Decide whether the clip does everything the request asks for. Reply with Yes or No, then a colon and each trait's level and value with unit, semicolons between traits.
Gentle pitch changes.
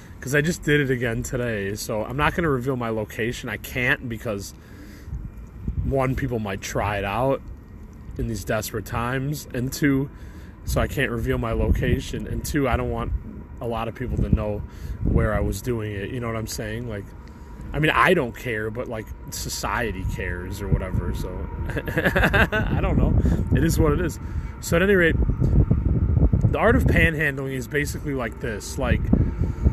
No: average, 4.2 semitones